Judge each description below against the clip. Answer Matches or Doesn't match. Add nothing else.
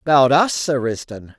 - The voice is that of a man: Matches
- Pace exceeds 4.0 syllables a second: Doesn't match